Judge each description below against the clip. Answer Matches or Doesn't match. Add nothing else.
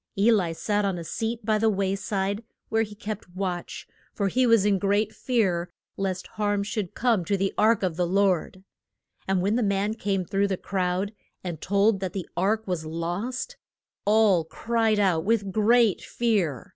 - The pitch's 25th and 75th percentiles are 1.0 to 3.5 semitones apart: Matches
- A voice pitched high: Matches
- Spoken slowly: Doesn't match